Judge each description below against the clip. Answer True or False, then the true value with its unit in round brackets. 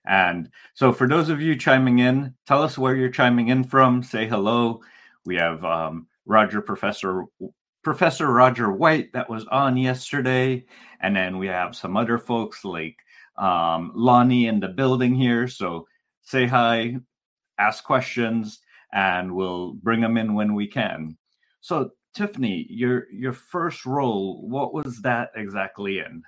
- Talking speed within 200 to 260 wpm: False (155 wpm)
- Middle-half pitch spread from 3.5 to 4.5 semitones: True (4.2 semitones)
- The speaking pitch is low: True (120 Hz)